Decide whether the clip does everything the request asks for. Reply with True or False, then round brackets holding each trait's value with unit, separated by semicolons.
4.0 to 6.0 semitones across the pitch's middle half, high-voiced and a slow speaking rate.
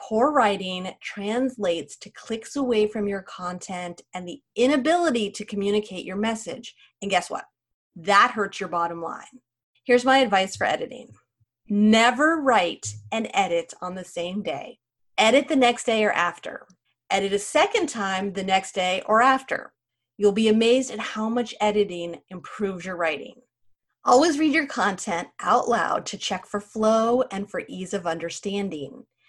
False (4.5 semitones; 200 Hz; 160 wpm)